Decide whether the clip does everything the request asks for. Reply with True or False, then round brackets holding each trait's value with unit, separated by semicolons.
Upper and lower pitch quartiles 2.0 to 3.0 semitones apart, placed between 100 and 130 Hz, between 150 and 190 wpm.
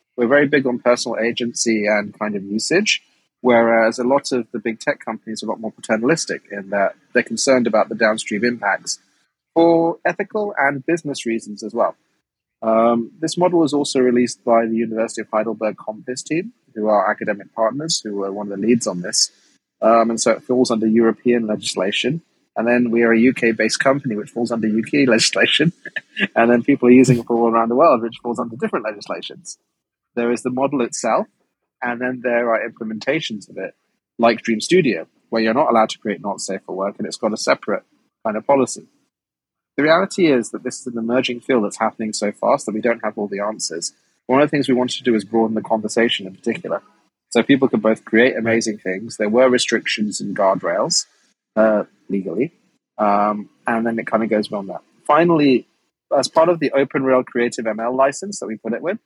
False (2.7 semitones; 115 Hz; 205 wpm)